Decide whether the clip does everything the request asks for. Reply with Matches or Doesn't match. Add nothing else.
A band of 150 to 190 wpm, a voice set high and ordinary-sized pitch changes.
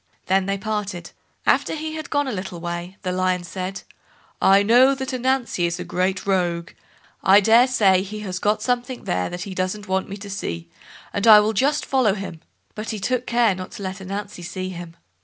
Doesn't match